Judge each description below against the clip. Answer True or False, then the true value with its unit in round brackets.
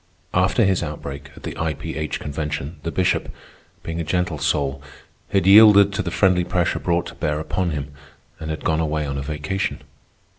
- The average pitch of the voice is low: True (80 Hz)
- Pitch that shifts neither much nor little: True (3.6 semitones)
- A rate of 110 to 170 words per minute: False (190 wpm)